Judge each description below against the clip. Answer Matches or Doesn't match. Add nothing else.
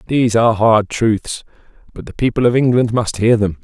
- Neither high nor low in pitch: Doesn't match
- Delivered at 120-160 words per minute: Doesn't match